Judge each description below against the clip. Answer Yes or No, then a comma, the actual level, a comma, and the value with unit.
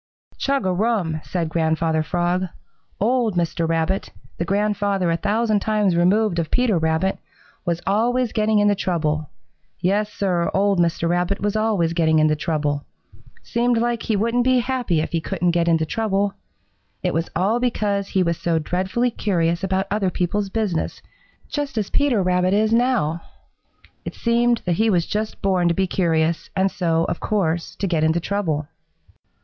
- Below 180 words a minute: Yes, average, 165 wpm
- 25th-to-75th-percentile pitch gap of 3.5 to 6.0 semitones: Yes, average, 4.2 semitones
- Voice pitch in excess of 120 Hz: Yes, high, 190 Hz